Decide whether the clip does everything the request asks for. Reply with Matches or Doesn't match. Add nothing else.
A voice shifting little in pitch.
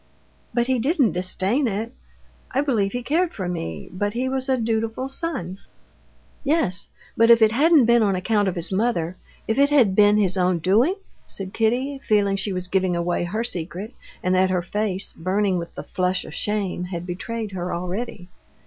Doesn't match